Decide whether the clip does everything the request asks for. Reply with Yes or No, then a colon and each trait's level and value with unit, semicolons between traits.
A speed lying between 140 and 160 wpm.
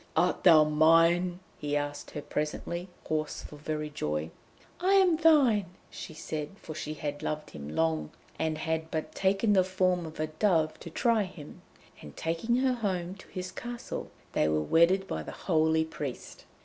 No: average, 175 wpm